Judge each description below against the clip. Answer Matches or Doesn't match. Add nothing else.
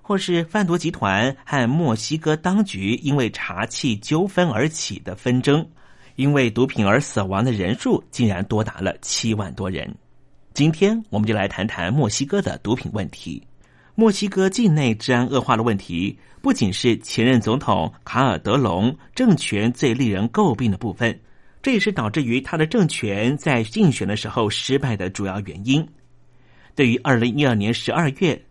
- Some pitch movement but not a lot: Doesn't match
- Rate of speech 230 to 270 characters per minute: Matches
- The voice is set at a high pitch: Doesn't match